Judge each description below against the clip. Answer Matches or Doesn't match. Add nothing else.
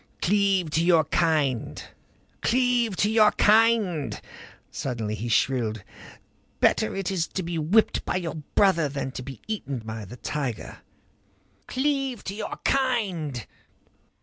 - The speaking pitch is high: Doesn't match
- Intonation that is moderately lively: Doesn't match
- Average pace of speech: Doesn't match